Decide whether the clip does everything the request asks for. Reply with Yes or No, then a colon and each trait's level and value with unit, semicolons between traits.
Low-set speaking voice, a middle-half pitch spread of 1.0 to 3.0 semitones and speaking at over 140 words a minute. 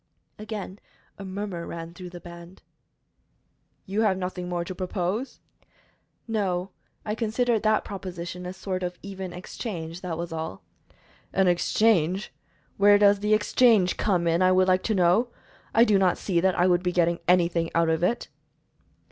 No: medium, 185 Hz; average, 2.7 semitones; average, 165 wpm